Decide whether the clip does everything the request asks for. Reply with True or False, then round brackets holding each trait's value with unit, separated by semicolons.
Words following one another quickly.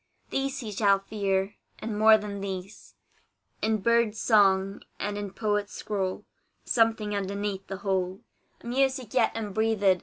False (140 wpm)